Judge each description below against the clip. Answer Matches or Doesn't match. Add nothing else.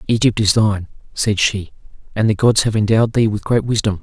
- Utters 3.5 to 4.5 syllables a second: Doesn't match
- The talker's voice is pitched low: Matches